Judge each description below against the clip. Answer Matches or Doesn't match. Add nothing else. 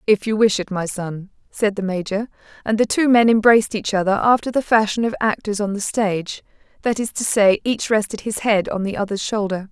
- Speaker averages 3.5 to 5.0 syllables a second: Doesn't match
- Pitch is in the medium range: Doesn't match